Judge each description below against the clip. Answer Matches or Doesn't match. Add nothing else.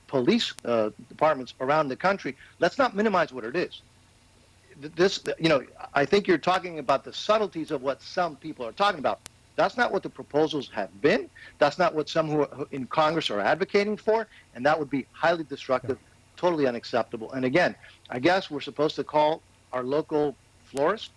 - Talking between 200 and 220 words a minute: Doesn't match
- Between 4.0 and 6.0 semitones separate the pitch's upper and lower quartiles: Matches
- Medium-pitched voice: Matches